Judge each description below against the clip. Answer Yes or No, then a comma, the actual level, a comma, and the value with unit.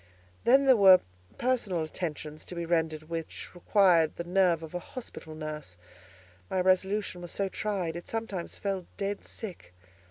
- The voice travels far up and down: No, average, 3.6 semitones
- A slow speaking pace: No, average, 155 wpm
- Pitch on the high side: No, medium, 180 Hz